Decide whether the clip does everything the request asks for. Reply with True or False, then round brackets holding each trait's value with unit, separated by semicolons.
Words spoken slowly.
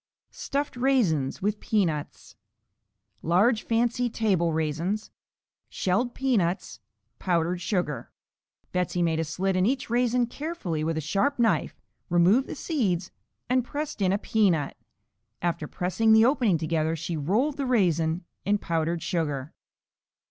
True (130 wpm)